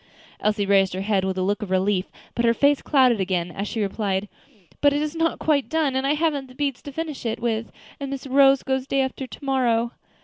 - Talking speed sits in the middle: No, fast, 235 wpm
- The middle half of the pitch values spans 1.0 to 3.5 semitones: No, wide, 5.5 semitones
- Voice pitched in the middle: No, very high, 255 Hz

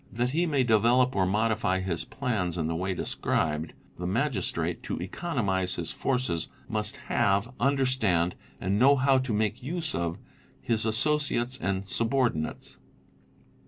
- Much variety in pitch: Yes, wide, 5.7 semitones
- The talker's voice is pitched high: No, low, 110 Hz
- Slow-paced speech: No, average, 145 wpm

